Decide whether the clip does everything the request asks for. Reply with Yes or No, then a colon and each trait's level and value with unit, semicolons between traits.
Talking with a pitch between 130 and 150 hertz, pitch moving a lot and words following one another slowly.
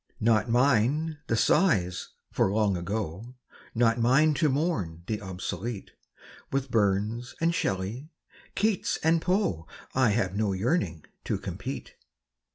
No: low, 115 Hz; wide, 6.6 semitones; slow, 125 wpm